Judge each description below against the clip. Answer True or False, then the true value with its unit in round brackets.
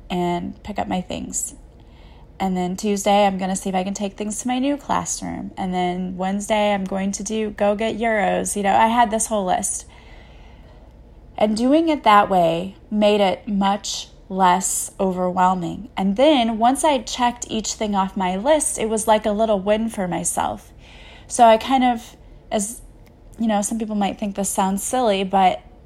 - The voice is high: True (205 Hz)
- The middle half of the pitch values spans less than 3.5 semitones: True (2.8 semitones)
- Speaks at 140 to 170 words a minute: False (190 wpm)